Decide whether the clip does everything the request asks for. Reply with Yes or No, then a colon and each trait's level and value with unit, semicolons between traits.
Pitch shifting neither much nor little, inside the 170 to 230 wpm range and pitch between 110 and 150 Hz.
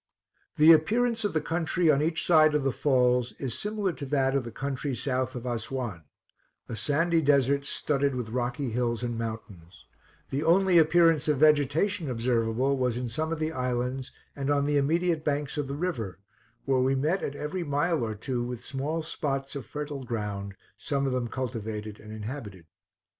Yes: average, 4.1 semitones; average, 180 wpm; low, 135 Hz